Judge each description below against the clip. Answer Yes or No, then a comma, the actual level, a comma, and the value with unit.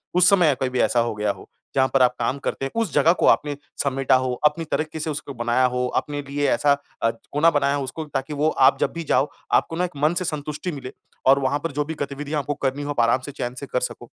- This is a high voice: No, medium, 140 Hz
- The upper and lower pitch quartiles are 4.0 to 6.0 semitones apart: No, narrow, 2.6 semitones